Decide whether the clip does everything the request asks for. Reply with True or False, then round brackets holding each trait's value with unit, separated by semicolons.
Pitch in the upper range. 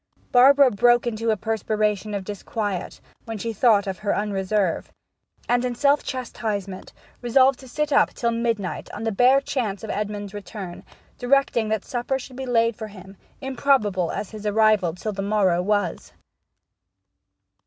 True (215 Hz)